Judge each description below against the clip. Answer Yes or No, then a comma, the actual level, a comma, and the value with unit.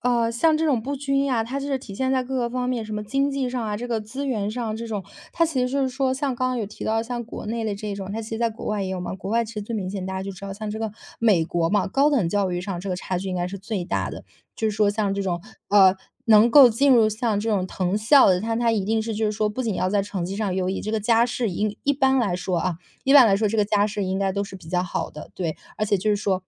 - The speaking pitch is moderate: No, high, 215 Hz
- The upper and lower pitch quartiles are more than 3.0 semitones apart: Yes, average, 3.8 semitones